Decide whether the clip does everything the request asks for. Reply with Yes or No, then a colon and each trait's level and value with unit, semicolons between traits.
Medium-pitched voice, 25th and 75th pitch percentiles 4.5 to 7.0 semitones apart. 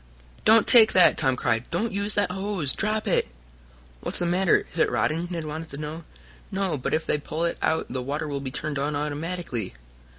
Yes: medium, 160 Hz; average, 4.8 semitones